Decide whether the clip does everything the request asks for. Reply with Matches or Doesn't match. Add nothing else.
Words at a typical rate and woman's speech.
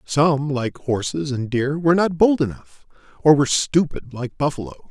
Doesn't match